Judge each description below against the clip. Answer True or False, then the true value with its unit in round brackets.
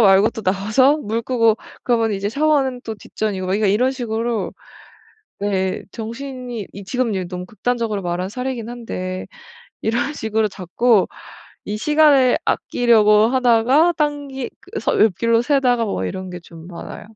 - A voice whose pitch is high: True (225 Hz)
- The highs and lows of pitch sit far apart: False (3.9 semitones)